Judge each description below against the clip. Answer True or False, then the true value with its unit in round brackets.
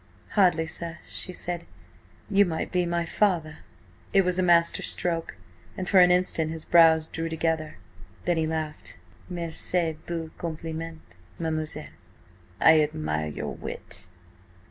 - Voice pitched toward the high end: False (165 Hz)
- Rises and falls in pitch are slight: True (1.8 semitones)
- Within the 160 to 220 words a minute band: False (135 wpm)